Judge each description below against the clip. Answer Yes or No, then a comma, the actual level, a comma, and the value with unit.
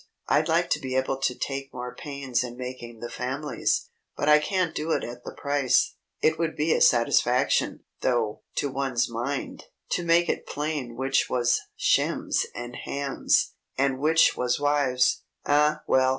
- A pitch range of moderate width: Yes, average, 3.0 semitones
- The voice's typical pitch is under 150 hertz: Yes, low, 135 Hz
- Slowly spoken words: No, average, 165 wpm